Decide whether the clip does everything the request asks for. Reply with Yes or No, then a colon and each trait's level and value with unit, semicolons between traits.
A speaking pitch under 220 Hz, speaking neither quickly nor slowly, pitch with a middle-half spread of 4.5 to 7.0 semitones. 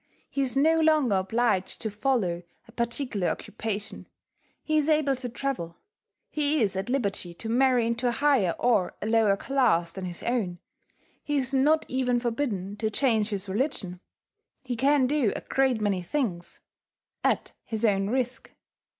No: high, 235 Hz; average, 160 wpm; average, 5.1 semitones